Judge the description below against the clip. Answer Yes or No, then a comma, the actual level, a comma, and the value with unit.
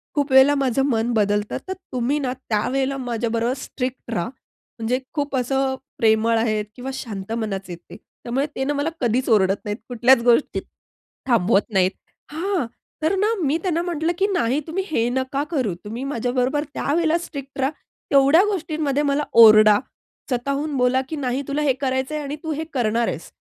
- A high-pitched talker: Yes, very high, 260 Hz